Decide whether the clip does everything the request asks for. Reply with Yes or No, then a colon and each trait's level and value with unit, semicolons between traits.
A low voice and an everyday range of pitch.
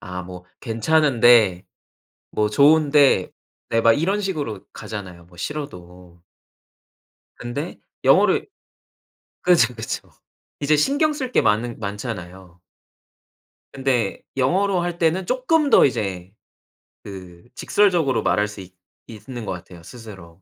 No: low, 115 Hz; wide, 8.5 semitones